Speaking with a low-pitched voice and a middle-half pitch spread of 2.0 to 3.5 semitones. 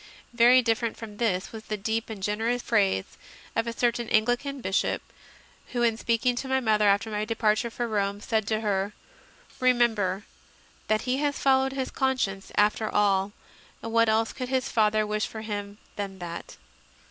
No: high, 220 Hz; narrow, 2.6 semitones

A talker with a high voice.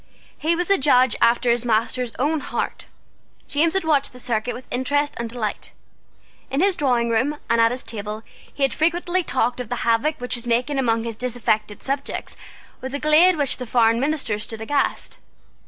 Yes: very high, 250 Hz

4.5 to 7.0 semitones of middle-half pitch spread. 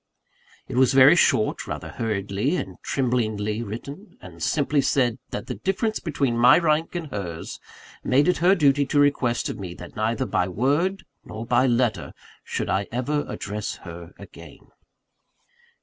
Yes: wide, 5.6 semitones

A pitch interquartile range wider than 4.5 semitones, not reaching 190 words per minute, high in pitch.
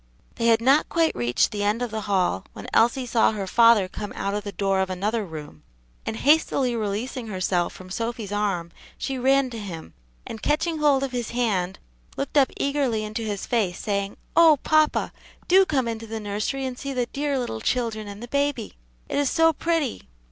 No: average, 5.0 semitones; average, 200 wpm; high, 230 Hz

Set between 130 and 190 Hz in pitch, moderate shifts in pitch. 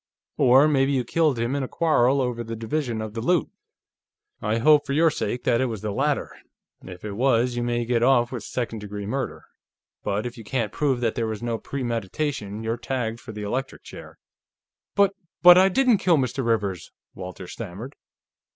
No: low, 120 Hz; average, 3.5 semitones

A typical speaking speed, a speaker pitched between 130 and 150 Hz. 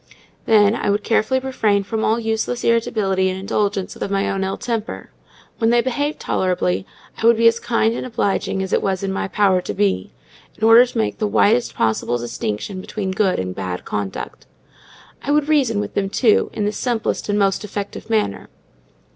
No: average, 190 wpm; high, 205 Hz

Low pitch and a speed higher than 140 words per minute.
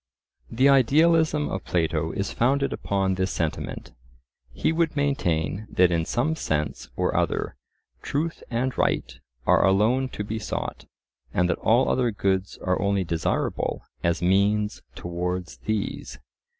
No: low, 100 Hz; slow, 135 wpm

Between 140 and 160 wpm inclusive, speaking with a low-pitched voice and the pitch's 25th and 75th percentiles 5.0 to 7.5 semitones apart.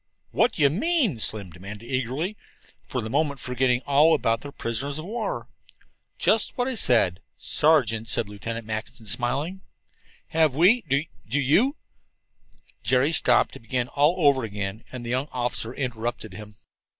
Yes: average, 155 wpm; low, 130 Hz; wide, 5.4 semitones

